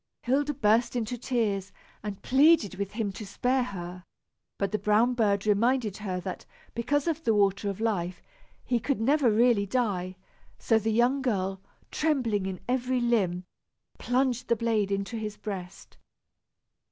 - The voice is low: No, high, 220 Hz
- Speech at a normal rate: Yes, average, 155 wpm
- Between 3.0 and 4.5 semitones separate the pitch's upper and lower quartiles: Yes, average, 3.8 semitones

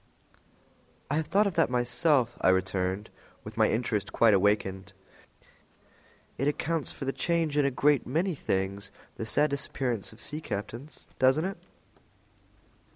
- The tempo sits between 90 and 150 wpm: Yes, average, 145 wpm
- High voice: No, low, 125 Hz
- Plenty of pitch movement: Yes, wide, 6.4 semitones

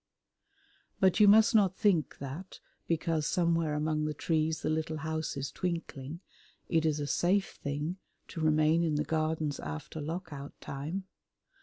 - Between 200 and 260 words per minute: No, average, 155 wpm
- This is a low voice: No, medium, 160 Hz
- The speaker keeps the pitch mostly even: Yes, narrow, 2.2 semitones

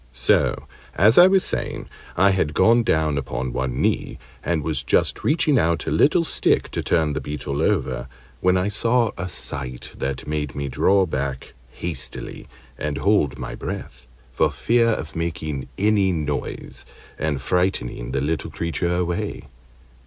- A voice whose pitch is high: No, very low, 80 Hz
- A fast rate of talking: No, average, 160 wpm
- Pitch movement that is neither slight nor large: No, wide, 5.8 semitones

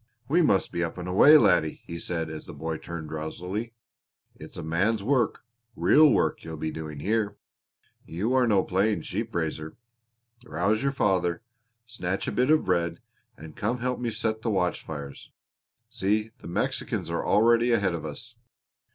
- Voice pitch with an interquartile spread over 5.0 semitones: Yes, wide, 5.6 semitones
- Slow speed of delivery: No, average, 170 wpm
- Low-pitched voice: Yes, very low, 95 Hz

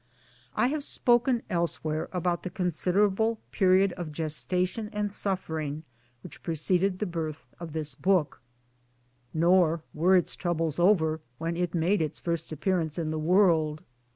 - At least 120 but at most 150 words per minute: Yes, average, 140 wpm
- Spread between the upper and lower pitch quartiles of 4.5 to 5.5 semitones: No, average, 3.1 semitones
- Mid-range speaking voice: Yes, medium, 175 Hz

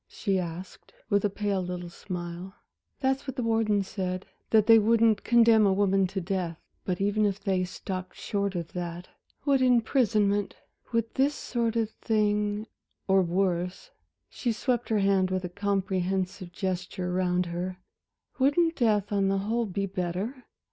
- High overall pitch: Yes, high, 200 Hz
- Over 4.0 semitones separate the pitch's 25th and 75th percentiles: No, average, 3.4 semitones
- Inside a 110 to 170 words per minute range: Yes, average, 155 wpm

